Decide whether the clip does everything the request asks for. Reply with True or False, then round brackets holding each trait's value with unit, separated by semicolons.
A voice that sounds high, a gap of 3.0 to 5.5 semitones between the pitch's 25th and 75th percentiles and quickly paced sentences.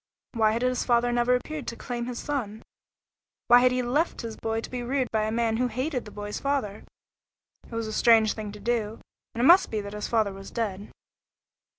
False (235 Hz; 2.5 semitones; 220 wpm)